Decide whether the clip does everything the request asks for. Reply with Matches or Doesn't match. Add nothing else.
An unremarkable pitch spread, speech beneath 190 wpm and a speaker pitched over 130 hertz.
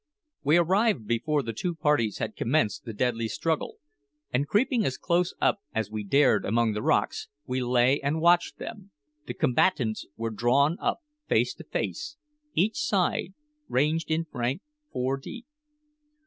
Doesn't match